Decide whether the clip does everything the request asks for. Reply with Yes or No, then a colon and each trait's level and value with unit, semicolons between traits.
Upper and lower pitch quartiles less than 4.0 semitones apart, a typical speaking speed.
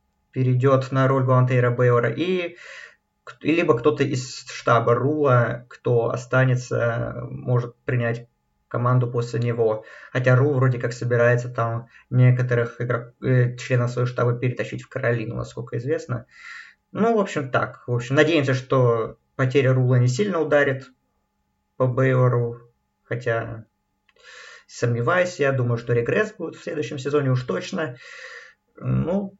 Yes: narrow, 2.4 semitones; average, 130 wpm